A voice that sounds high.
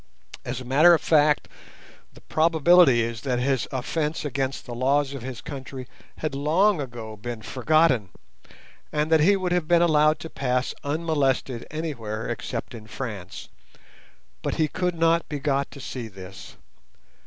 No: medium, 140 Hz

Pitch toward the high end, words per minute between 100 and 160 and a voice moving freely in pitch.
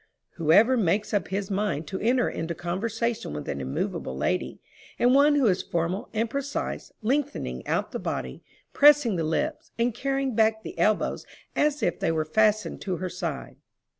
No: high, 215 Hz; average, 175 wpm; wide, 6.5 semitones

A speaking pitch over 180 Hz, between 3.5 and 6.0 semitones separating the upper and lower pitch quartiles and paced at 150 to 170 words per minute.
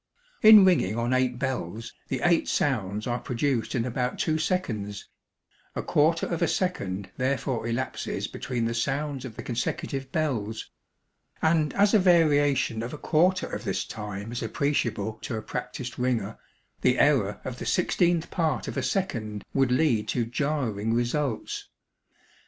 No: low, 125 Hz; average, 5.0 semitones; average, 155 wpm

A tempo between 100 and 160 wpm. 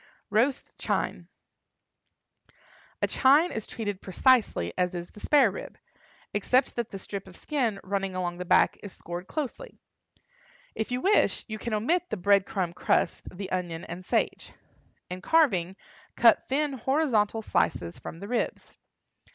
Yes: average, 150 wpm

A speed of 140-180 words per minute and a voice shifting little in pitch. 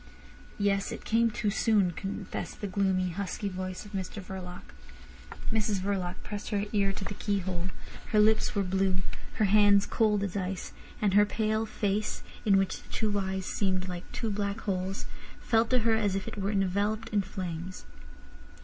Yes: average, 175 wpm; narrow, 1.9 semitones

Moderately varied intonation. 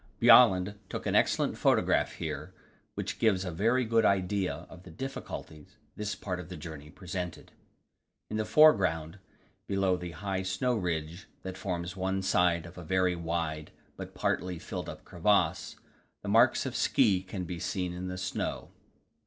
No: narrow, 2.3 semitones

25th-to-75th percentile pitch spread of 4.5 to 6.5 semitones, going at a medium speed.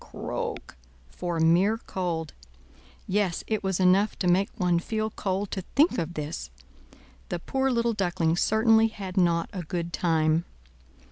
No: average, 3.8 semitones; average, 145 wpm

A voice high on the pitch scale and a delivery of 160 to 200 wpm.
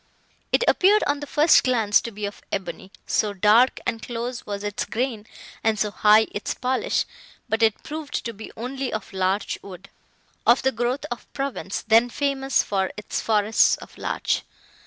Yes: high, 225 Hz; average, 175 wpm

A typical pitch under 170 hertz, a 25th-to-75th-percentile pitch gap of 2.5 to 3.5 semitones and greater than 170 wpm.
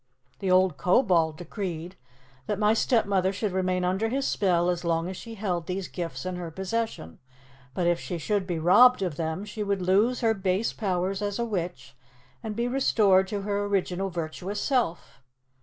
No: high, 190 Hz; average, 2.9 semitones; average, 180 wpm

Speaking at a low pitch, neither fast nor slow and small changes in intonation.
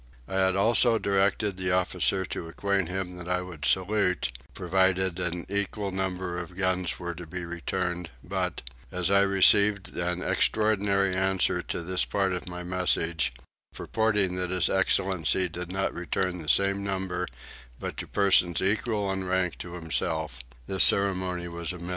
Yes: very low, 95 Hz; average, 160 wpm; narrow, 1.7 semitones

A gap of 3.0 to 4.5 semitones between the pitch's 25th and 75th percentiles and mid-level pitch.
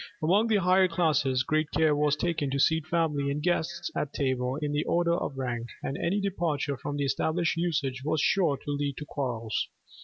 Yes: average, 3.5 semitones; medium, 150 Hz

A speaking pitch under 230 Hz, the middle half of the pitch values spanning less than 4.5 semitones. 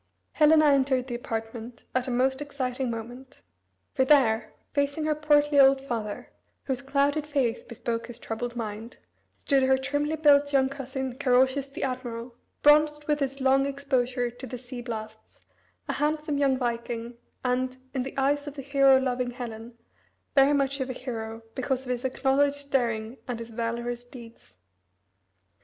No: very high, 260 Hz; average, 2.7 semitones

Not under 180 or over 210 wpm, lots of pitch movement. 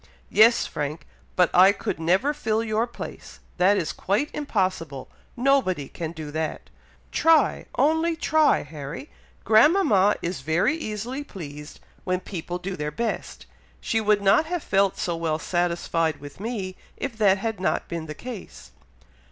No: average, 150 wpm; wide, 6.0 semitones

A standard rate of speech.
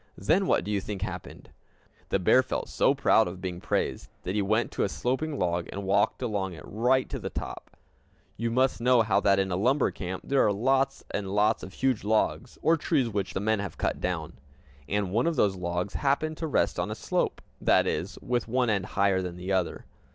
No: fast, 215 wpm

